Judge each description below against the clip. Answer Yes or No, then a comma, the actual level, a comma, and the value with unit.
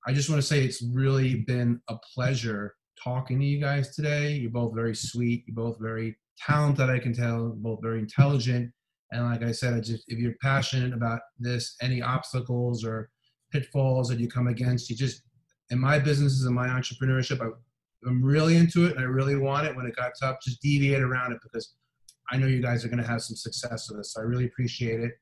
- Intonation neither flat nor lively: No, narrow, 2.2 semitones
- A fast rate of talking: Yes, fast, 220 wpm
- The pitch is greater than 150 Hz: No, low, 125 Hz